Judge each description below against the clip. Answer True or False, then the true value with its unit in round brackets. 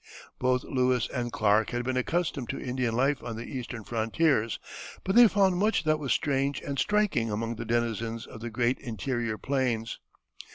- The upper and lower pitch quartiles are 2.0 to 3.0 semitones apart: False (3.4 semitones)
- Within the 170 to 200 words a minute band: True (175 wpm)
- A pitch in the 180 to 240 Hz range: False (125 Hz)